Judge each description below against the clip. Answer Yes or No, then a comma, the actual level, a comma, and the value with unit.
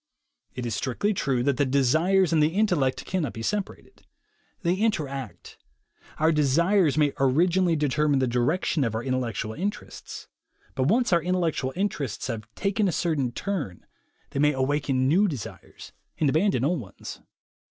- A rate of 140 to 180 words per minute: Yes, average, 155 wpm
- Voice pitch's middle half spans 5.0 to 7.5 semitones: Yes, wide, 5.6 semitones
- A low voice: No, medium, 150 Hz